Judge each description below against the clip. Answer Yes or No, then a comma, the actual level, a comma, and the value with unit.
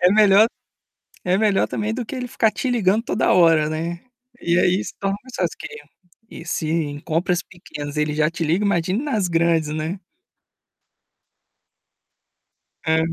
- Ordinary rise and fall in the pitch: Yes, average, 4.5 semitones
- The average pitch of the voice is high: No, medium, 180 Hz